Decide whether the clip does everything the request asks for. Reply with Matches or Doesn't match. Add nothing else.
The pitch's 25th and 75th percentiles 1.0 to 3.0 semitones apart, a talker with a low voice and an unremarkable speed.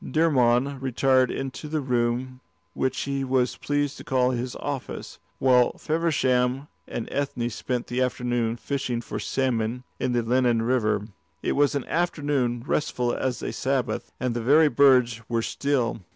Matches